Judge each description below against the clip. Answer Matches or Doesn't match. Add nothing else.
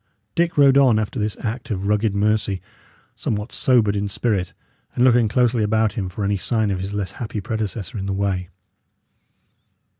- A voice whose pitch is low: Matches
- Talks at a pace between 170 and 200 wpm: Matches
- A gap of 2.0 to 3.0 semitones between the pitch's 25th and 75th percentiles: Matches